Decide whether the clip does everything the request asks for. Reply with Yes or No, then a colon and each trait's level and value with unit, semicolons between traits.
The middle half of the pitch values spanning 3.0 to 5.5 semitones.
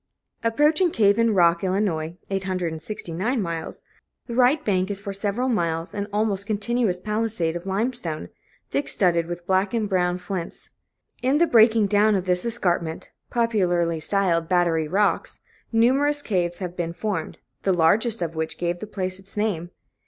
Yes: average, 4.3 semitones